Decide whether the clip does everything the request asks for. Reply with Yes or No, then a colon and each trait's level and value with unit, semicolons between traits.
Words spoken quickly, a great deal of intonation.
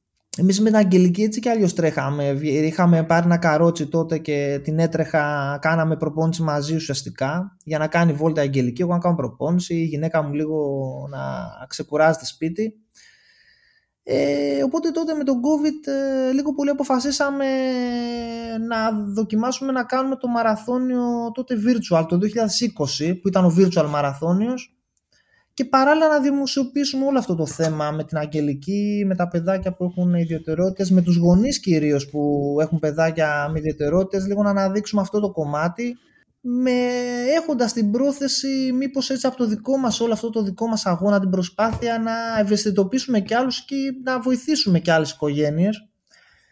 No: average, 155 wpm; wide, 7.6 semitones